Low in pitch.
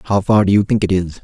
Yes: low, 100 Hz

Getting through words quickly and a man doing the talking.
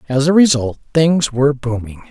No: average, 170 wpm; male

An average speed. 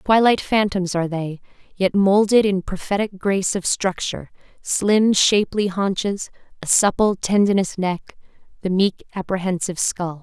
No: slow, 130 wpm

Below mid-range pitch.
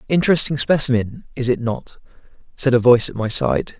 Yes: low, 130 Hz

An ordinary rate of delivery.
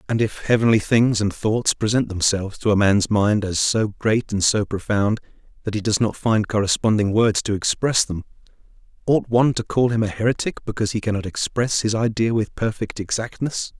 Yes: average, 190 wpm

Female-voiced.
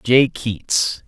No: male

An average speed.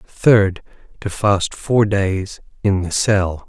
No: slow, 120 wpm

